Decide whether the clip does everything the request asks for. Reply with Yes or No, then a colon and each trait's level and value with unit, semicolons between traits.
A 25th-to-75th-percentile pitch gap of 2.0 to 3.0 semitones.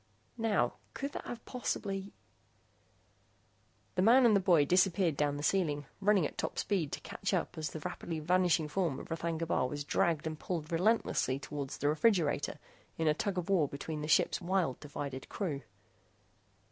No: average, 4.5 semitones